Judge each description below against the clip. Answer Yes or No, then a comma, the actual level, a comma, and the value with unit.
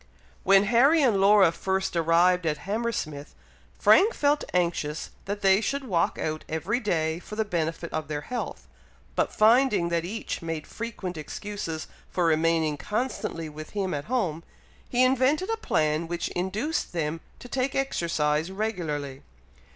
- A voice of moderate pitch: Yes, medium, 180 Hz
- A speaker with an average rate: Yes, average, 150 wpm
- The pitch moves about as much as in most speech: No, wide, 5.9 semitones